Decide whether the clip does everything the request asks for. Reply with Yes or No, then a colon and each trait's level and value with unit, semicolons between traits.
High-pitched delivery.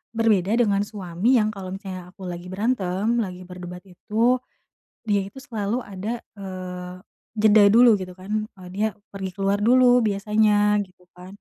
Yes: high, 200 Hz